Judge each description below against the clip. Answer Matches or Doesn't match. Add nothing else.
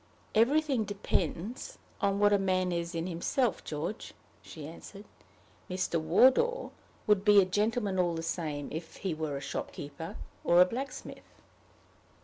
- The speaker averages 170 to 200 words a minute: Doesn't match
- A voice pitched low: Doesn't match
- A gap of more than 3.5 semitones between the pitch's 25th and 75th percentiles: Matches